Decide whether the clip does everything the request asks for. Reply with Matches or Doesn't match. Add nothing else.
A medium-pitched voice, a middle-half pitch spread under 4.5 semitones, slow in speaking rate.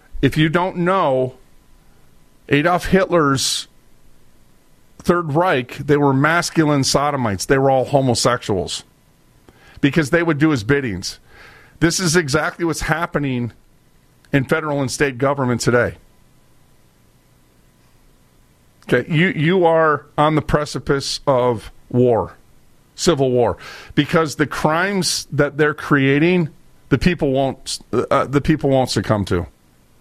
Matches